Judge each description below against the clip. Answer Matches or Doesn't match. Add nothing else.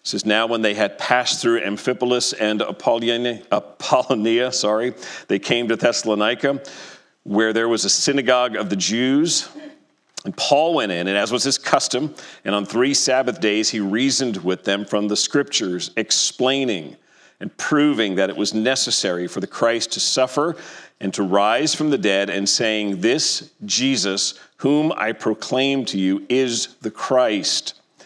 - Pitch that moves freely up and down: Doesn't match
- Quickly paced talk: Doesn't match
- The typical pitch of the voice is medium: Doesn't match